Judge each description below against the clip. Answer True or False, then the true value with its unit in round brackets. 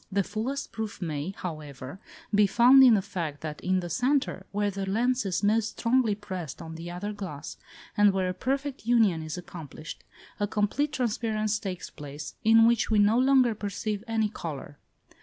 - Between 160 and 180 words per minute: True (175 wpm)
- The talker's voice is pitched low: False (205 Hz)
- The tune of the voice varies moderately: True (4.4 semitones)